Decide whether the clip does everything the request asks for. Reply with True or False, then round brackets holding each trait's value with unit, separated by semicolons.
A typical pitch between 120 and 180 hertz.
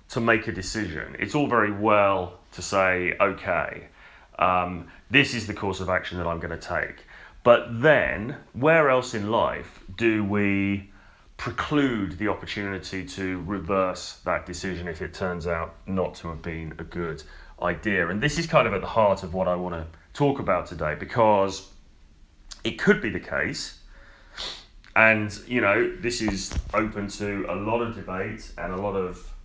False (95 Hz)